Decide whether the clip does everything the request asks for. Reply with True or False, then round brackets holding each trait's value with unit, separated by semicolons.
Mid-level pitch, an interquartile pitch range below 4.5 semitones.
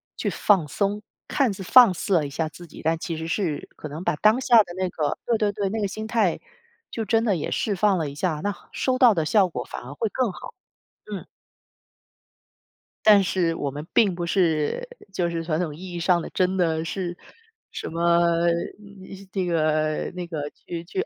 True (175 Hz; 4.0 semitones)